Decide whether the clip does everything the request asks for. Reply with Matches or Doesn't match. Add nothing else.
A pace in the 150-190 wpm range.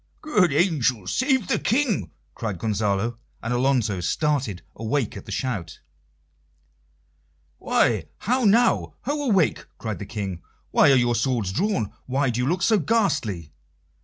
Doesn't match